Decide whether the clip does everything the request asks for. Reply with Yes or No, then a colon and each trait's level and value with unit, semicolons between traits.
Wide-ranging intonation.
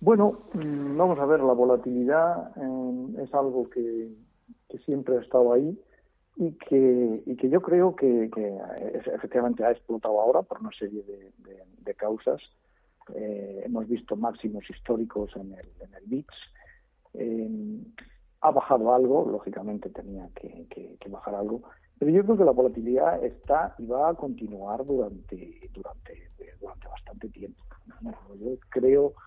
Yes: wide, 5.9 semitones